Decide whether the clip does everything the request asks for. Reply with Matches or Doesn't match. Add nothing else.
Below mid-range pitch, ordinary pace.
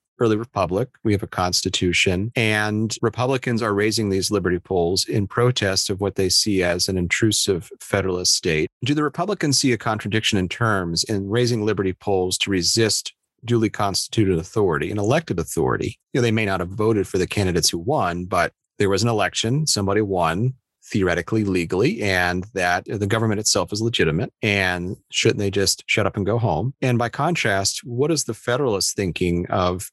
Matches